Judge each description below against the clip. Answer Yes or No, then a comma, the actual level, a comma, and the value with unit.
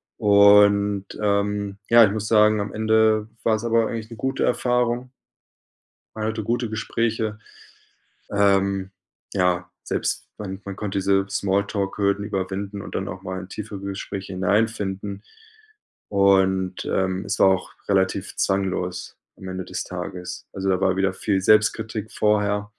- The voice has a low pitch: Yes, low, 100 Hz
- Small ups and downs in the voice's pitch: Yes, narrow, 2.0 semitones